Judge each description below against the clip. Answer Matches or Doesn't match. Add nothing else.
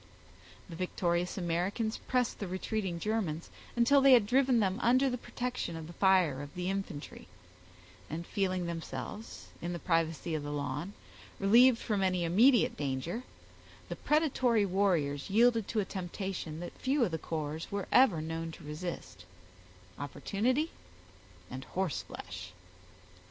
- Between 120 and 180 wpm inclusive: Matches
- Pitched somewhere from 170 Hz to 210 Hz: Matches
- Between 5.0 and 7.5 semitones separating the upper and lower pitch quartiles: Matches